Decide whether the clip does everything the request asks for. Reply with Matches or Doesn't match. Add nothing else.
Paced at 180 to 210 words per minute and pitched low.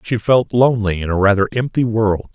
Matches